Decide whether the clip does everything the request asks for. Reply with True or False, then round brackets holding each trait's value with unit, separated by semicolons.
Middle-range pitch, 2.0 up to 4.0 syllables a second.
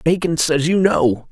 True (155 Hz; 3.9 syllables/s)